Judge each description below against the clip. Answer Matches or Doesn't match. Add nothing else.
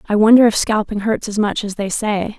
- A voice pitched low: Doesn't match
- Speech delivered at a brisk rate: Matches